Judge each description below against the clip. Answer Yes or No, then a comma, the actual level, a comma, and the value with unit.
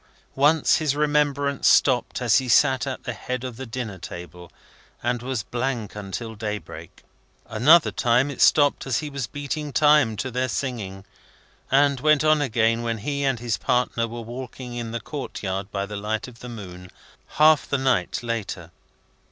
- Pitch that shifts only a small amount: No, average, 4.1 semitones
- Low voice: Yes, low, 125 Hz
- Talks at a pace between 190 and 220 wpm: No, average, 175 wpm